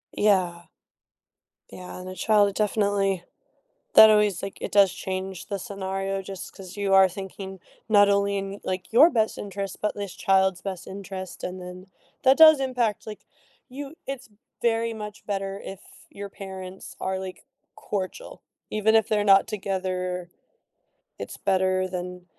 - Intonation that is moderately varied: No, narrow, 2.0 semitones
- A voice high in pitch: Yes, high, 195 Hz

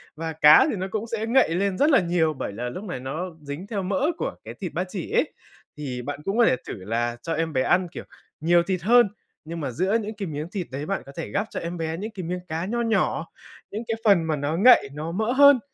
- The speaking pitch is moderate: Yes, medium, 175 Hz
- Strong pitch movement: Yes, wide, 5.7 semitones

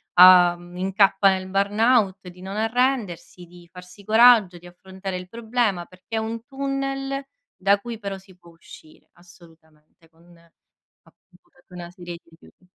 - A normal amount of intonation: Yes, average, 4.0 semitones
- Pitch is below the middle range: No, high, 190 Hz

